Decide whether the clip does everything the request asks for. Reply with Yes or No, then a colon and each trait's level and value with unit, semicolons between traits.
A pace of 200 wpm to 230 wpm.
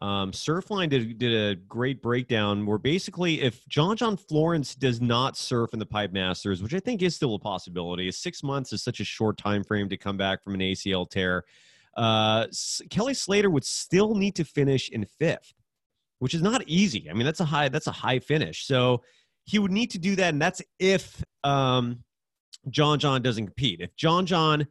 Yes: fast, 205 wpm